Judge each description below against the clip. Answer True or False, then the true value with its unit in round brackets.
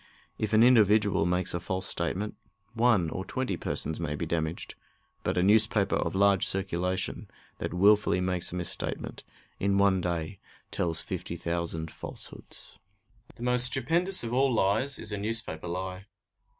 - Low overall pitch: True (95 Hz)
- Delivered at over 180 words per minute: False (150 wpm)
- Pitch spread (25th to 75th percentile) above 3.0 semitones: True (4.0 semitones)